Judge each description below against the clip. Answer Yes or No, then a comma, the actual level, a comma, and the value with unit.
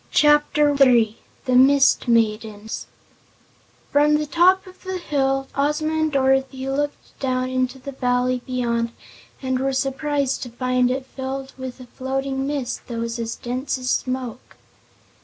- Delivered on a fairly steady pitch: Yes, narrow, 2.1 semitones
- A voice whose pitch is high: Yes, very high, 265 Hz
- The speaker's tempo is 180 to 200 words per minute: No, average, 145 wpm